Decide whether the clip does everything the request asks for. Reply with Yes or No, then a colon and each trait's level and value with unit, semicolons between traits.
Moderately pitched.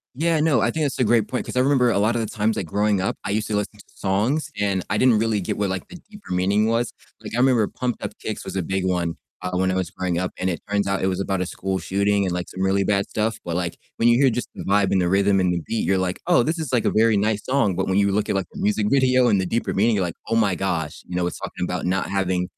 No: low, 100 Hz